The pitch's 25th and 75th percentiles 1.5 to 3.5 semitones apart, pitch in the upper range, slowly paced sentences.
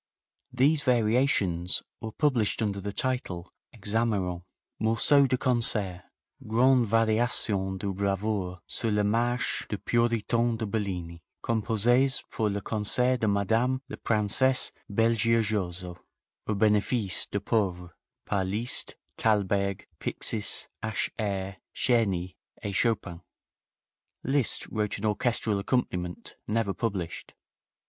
No: average, 3.1 semitones; low, 110 Hz; slow, 110 wpm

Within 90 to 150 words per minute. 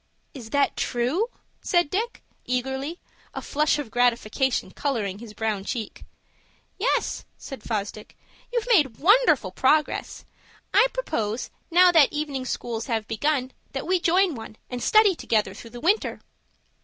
Yes: average, 140 wpm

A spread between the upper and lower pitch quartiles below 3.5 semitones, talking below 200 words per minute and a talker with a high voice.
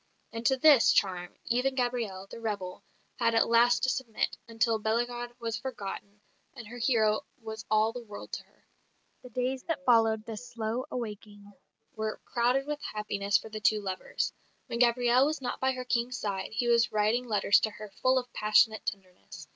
Yes: narrow, 2.6 semitones; average, 180 wpm; high, 230 Hz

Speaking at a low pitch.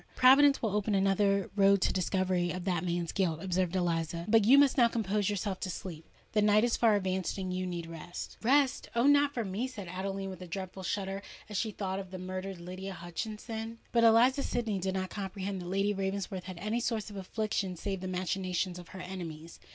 No: high, 195 Hz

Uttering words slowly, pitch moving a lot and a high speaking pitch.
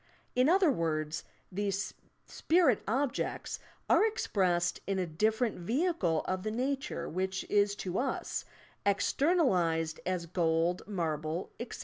Yes: slow, 125 wpm; wide, 6.8 semitones; high, 195 Hz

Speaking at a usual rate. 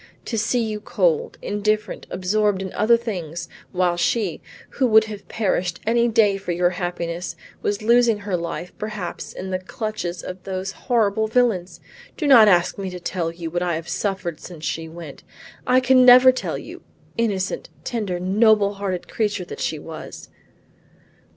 Yes: average, 165 wpm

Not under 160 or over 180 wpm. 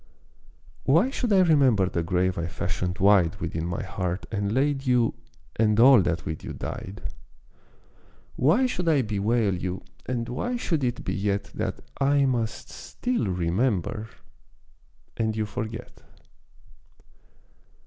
No: slow, 135 wpm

